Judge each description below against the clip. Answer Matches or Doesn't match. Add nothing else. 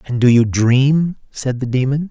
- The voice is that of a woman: Doesn't match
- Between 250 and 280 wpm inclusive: Doesn't match